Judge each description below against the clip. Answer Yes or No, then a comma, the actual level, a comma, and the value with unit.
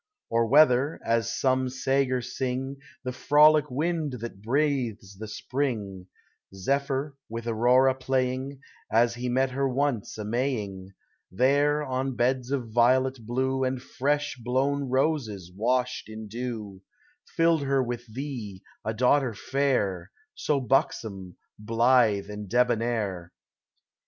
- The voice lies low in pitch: Yes, low, 125 Hz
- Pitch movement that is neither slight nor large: Yes, average, 3.4 semitones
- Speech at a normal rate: No, slow, 125 wpm